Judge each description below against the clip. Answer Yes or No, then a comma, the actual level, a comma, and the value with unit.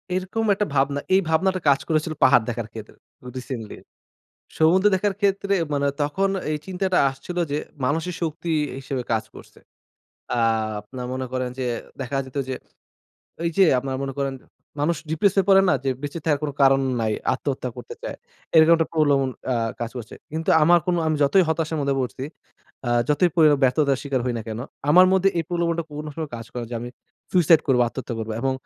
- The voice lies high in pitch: No, medium, 145 Hz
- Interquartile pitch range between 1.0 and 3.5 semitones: No, average, 4.6 semitones